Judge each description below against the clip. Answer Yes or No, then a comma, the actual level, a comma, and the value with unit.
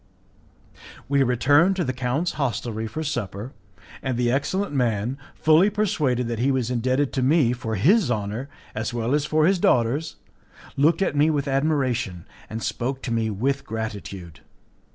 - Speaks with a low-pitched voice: Yes, low, 130 Hz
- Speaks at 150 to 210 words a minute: Yes, average, 160 wpm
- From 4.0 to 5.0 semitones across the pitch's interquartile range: Yes, average, 4.3 semitones